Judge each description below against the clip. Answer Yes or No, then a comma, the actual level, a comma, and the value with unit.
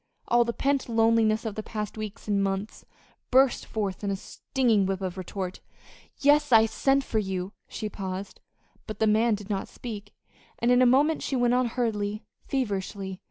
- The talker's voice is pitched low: No, high, 215 Hz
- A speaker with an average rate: Yes, average, 180 wpm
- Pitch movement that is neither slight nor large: Yes, average, 3.4 semitones